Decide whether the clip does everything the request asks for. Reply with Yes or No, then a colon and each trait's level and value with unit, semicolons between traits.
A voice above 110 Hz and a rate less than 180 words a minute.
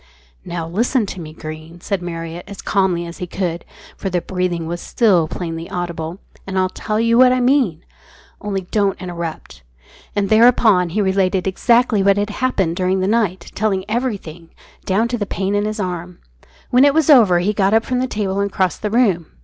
No: high, 190 Hz; average, 200 wpm